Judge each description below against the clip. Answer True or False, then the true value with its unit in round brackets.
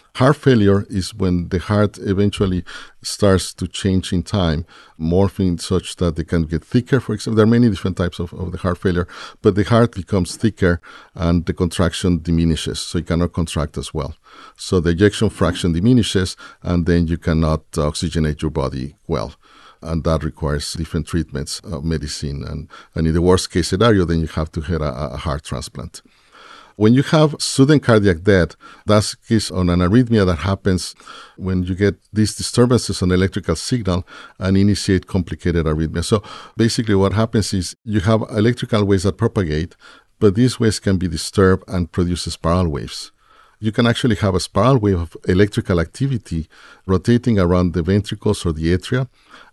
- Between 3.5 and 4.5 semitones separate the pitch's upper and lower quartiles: True (3.9 semitones)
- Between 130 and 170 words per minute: False (180 wpm)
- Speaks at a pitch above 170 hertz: False (95 Hz)